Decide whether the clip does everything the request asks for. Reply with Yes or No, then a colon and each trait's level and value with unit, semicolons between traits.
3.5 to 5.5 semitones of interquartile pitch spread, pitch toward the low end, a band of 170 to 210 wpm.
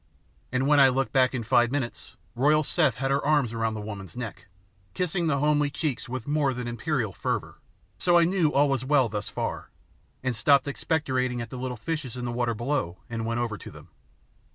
Yes: average, 3.8 semitones; low, 130 Hz; fast, 205 wpm